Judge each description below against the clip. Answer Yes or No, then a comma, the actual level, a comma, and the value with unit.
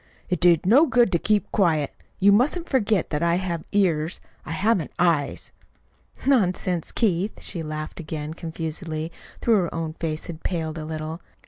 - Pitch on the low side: No, medium, 170 Hz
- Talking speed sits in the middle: Yes, average, 165 wpm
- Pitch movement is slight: No, average, 4.1 semitones